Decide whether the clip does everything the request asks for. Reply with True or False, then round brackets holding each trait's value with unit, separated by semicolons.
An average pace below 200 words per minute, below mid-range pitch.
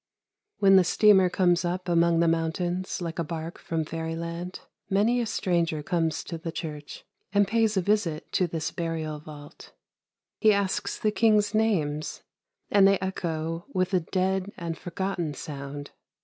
False (160 wpm; 175 Hz)